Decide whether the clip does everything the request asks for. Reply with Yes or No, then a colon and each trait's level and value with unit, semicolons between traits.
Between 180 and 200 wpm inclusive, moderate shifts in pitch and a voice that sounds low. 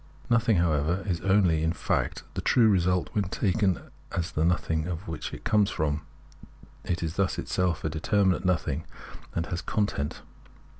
No: average, 165 wpm; average, 3.3 semitones; very low, 90 Hz